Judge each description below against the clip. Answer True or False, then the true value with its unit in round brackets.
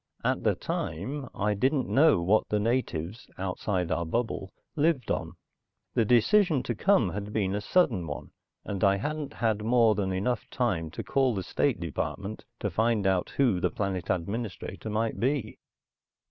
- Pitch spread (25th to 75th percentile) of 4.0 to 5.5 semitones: True (4.7 semitones)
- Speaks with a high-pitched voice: False (110 Hz)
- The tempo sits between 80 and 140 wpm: False (165 wpm)